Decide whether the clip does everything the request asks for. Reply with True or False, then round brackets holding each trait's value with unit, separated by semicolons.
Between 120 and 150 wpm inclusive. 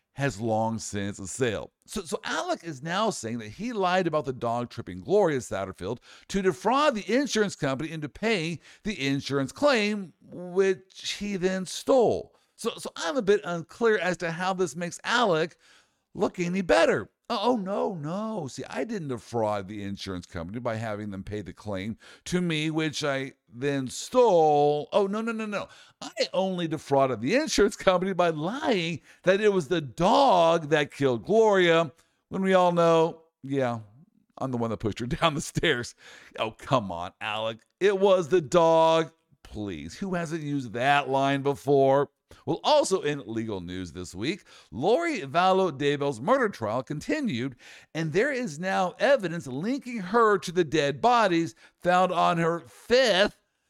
False (165 wpm)